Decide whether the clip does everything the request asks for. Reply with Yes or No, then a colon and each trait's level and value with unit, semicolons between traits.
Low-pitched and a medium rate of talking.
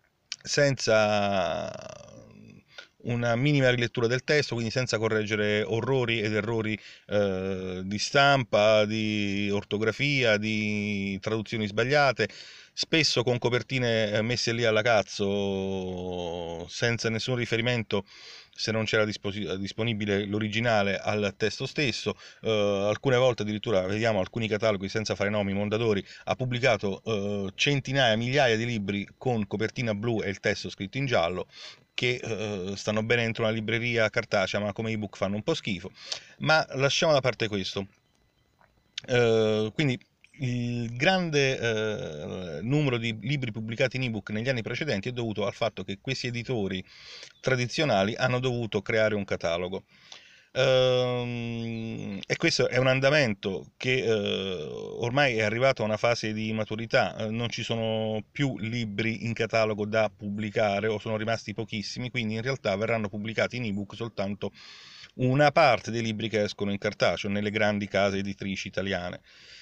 Yes: low, 110 Hz; average, 140 wpm